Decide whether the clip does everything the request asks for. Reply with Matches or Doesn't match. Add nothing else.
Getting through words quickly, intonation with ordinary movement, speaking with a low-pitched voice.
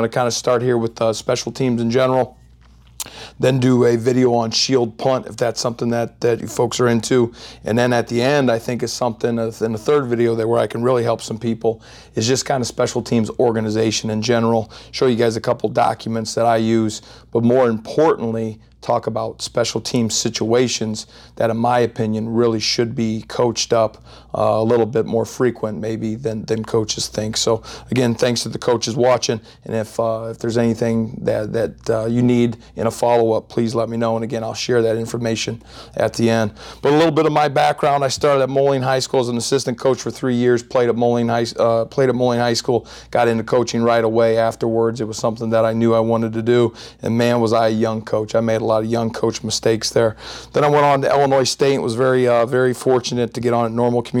Doesn't match